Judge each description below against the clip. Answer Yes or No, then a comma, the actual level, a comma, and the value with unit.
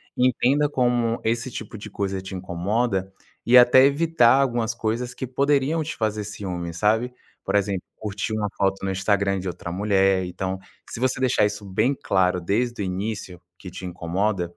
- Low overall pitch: Yes, low, 105 Hz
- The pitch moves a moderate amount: Yes, average, 4.3 semitones